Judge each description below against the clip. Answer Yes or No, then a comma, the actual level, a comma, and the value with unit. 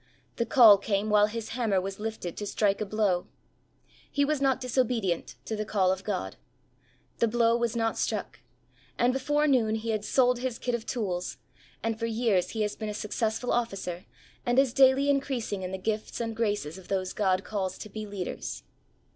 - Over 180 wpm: Yes, average, 190 wpm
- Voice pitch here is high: Yes, high, 220 Hz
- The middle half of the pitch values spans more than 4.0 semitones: No, average, 3.4 semitones